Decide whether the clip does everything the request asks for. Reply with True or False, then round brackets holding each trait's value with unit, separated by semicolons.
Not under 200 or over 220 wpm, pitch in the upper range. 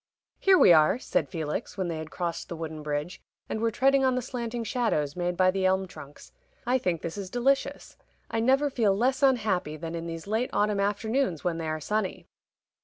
True (205 wpm; 195 Hz)